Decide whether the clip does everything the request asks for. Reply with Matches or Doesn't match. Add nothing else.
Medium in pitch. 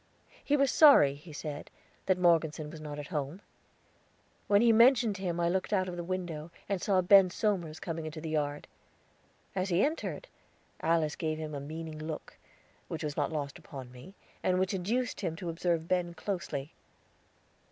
Matches